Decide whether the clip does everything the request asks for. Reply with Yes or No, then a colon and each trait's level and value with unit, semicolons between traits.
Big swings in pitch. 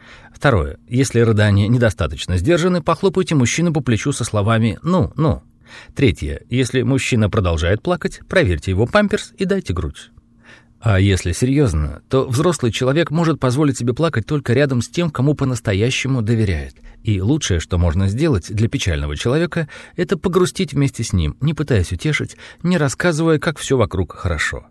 Yes: wide, 7.4 semitones